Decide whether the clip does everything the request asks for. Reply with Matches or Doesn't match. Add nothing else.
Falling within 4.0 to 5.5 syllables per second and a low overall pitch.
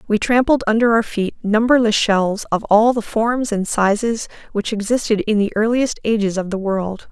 Doesn't match